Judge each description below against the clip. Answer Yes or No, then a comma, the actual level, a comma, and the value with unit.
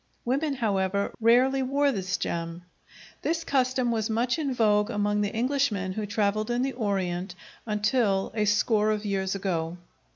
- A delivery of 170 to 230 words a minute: No, average, 155 wpm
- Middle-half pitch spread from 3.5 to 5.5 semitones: Yes, average, 4.1 semitones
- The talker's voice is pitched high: Yes, high, 215 Hz